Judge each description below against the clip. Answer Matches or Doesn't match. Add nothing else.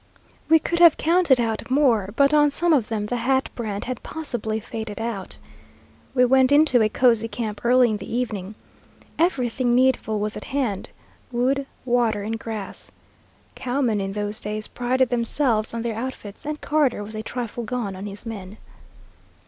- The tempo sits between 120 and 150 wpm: Doesn't match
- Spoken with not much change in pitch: Doesn't match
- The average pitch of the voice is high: Matches